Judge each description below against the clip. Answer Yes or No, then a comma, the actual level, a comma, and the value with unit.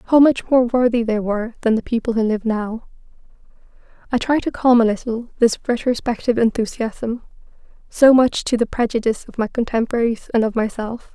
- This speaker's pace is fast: No, average, 170 wpm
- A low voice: No, high, 230 Hz